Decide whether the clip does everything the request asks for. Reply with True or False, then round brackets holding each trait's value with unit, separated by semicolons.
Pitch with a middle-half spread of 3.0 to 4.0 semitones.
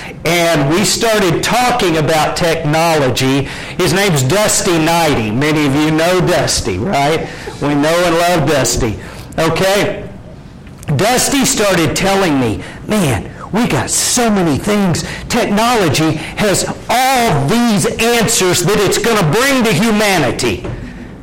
False (4.8 semitones)